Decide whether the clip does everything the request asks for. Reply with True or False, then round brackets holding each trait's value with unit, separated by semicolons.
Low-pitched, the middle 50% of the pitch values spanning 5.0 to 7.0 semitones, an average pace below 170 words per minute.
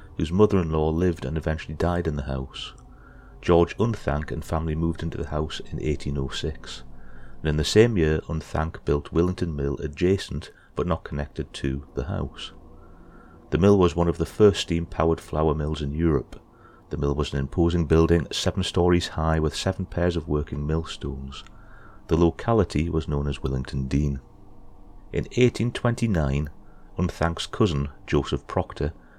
False (80 Hz; 3.4 semitones; 160 wpm)